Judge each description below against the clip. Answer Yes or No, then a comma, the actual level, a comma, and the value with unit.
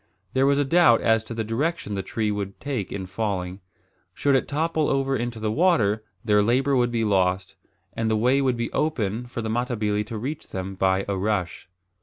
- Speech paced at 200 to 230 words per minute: Yes, fast, 205 wpm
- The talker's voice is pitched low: Yes, low, 115 Hz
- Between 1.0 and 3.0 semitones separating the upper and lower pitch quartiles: No, average, 4.8 semitones